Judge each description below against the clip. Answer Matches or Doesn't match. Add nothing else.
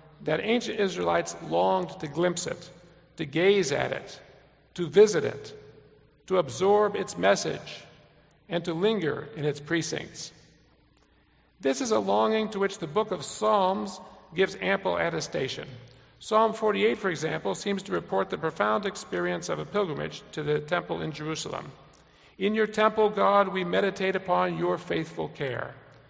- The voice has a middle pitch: Matches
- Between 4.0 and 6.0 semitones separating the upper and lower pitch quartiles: Matches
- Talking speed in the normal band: Matches